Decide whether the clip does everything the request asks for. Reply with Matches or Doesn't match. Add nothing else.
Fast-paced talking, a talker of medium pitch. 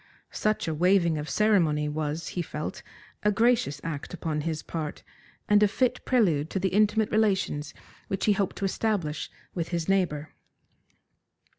Doesn't match